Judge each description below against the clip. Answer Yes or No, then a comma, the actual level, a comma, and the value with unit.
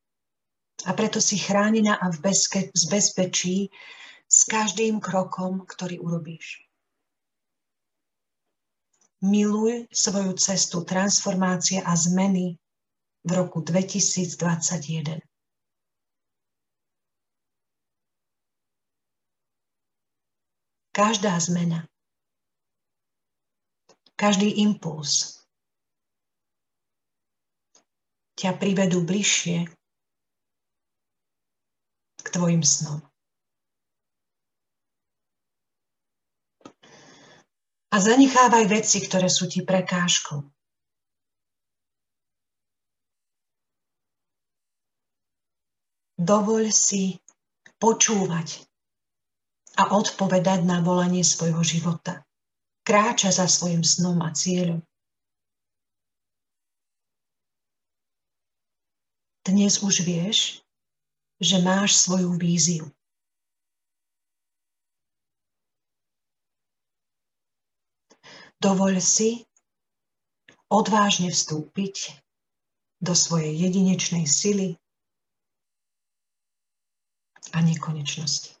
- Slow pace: Yes, slow, 55 wpm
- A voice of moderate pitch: Yes, medium, 180 Hz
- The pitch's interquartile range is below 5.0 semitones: Yes, average, 3.0 semitones